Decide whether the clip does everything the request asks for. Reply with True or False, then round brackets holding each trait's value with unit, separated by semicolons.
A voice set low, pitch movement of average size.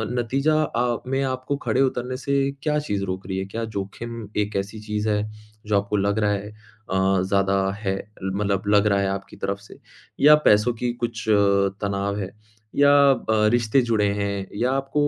True (105 Hz; 3.7 semitones)